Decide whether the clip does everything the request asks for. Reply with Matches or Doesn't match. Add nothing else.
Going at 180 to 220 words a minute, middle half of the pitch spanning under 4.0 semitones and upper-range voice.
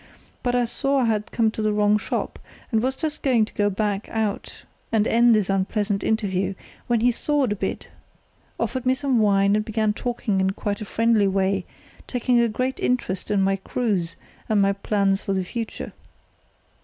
Matches